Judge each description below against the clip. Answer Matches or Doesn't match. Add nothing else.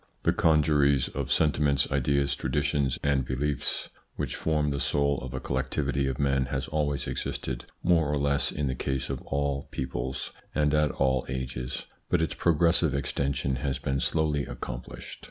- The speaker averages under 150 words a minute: Doesn't match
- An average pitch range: Doesn't match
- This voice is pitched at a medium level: Doesn't match